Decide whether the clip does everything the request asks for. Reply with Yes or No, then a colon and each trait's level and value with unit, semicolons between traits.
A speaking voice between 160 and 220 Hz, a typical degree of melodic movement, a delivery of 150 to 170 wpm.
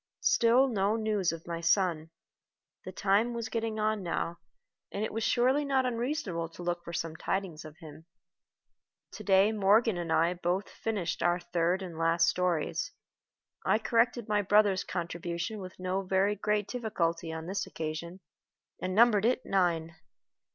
Yes: high, 190 Hz; average, 4.2 semitones; average, 160 wpm